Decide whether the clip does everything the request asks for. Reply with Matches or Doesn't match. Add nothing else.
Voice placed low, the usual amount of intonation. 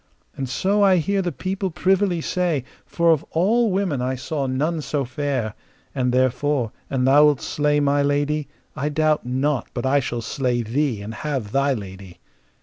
Doesn't match